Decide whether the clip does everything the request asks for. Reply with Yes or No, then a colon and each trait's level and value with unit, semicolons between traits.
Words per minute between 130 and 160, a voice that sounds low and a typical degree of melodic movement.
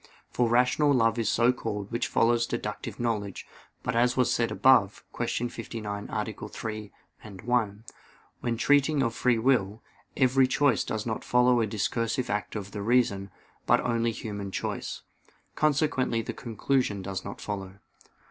Yes: average, 155 wpm; low, 115 Hz; average, 3.0 semitones